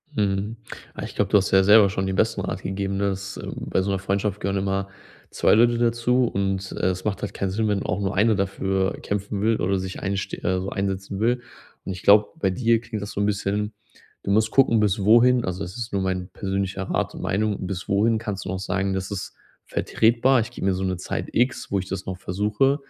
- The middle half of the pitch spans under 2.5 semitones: Yes, narrow, 2.1 semitones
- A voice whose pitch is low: Yes, low, 100 Hz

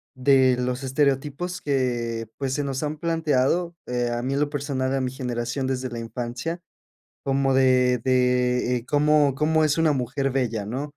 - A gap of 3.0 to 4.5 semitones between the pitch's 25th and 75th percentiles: No, narrow, 2.6 semitones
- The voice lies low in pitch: Yes, low, 130 Hz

